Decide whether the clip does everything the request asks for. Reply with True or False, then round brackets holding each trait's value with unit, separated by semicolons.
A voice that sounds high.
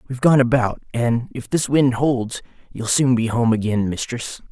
False (120 Hz)